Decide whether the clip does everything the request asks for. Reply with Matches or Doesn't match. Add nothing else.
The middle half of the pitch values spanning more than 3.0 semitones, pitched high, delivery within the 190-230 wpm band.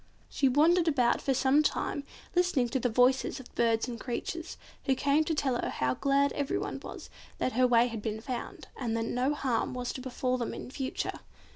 Doesn't match